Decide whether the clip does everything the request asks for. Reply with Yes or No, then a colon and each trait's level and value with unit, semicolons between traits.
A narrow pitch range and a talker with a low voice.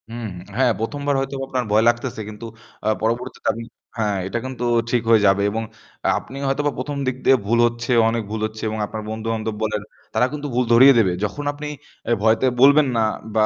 No: average, 3.1 semitones; low, 115 Hz